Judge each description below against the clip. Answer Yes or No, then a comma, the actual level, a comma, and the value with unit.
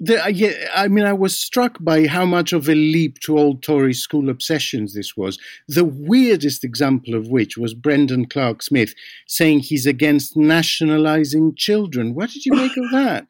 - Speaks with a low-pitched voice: No, medium, 155 Hz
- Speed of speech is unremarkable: Yes, average, 170 wpm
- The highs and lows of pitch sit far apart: Yes, wide, 5.7 semitones